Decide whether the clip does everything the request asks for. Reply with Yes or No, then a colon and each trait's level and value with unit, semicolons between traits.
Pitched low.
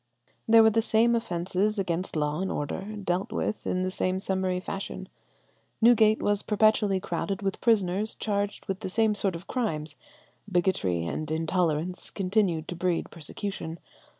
No: high, 190 Hz